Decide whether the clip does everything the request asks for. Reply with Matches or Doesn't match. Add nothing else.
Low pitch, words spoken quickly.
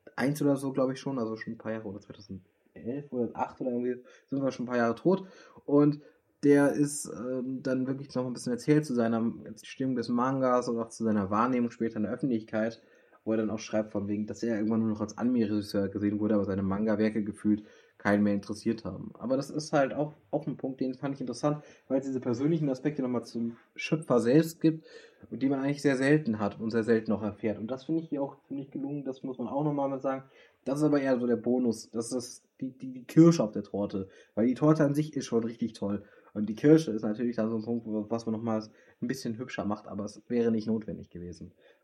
Matches